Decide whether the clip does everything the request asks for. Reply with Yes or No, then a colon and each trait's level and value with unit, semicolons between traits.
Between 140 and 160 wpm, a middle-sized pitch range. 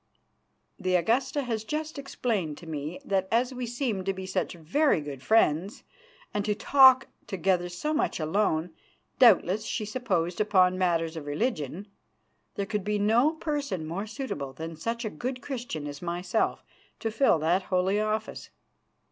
No: average, 155 wpm; wide, 5.9 semitones